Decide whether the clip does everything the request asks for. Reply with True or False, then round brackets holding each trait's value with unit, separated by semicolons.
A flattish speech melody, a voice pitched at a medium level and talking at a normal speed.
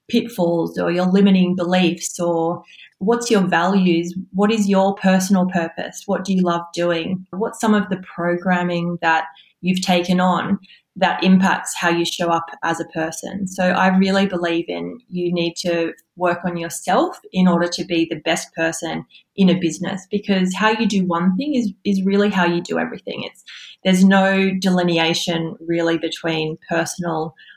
True (2.2 semitones; 180 Hz; 170 wpm)